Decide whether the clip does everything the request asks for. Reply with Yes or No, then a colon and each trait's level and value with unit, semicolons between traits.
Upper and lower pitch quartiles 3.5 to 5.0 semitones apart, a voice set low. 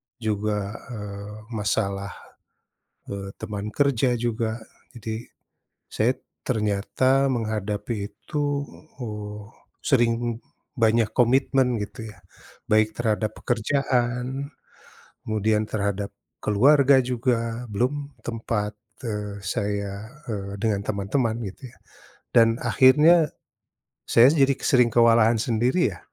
No: average, 3.1 semitones; low, 115 Hz